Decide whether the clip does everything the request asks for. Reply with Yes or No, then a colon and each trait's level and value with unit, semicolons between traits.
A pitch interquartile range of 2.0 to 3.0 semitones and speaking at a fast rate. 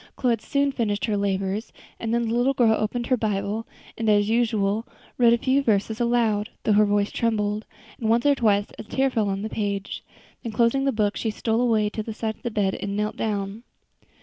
Yes: narrow, 2.4 semitones; fast, 220 wpm